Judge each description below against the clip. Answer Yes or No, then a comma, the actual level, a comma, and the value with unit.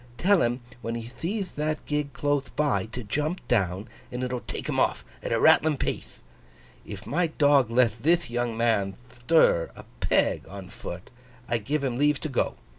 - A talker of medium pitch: No, low, 125 Hz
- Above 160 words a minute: Yes, average, 185 wpm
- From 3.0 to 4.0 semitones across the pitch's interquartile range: No, average, 4.4 semitones